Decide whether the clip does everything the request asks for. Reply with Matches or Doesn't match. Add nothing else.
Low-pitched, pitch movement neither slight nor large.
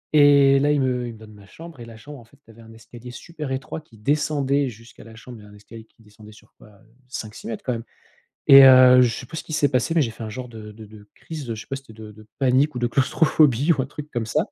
Matches